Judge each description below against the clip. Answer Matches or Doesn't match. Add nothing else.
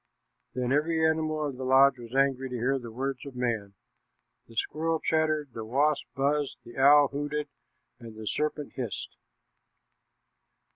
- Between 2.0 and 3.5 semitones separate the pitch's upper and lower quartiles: Matches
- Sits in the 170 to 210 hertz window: Doesn't match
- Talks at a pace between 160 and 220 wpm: Doesn't match